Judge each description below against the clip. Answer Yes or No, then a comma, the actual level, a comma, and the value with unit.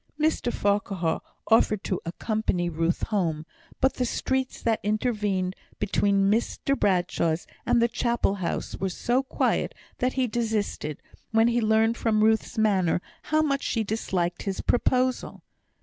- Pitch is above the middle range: Yes, high, 215 Hz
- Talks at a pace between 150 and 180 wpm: No, average, 140 wpm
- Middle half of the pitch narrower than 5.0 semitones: Yes, average, 4.0 semitones